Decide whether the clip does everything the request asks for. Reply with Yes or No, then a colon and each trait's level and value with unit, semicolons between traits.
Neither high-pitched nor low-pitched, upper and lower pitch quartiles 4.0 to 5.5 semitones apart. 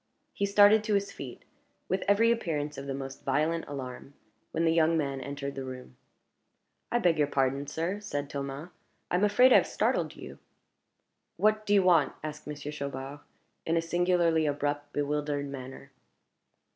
Yes: medium, 150 Hz; average, 4.3 semitones